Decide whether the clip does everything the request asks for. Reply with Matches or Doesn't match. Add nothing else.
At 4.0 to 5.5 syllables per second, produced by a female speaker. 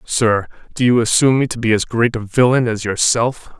Doesn't match